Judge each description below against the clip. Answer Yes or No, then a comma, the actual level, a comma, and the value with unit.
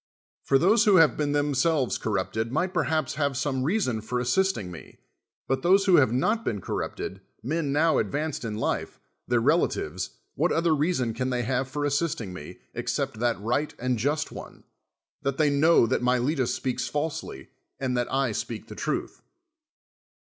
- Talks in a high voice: No, low, 135 Hz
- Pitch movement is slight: No, average, 4.4 semitones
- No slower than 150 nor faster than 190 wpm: Yes, average, 170 wpm